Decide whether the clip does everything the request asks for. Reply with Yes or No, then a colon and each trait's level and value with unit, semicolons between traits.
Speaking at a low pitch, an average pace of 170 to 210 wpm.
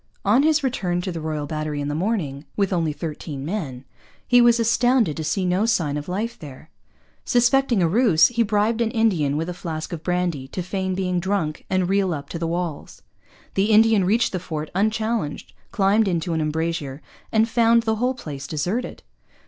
No: medium, 185 Hz; average, 190 wpm